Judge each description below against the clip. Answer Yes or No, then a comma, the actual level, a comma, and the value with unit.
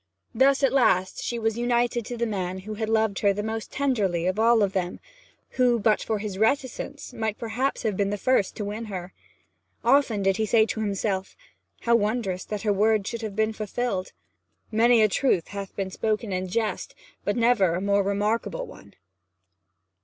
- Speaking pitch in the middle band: No, high, 215 Hz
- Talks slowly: No, average, 185 wpm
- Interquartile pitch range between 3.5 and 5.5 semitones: No, average, 2.9 semitones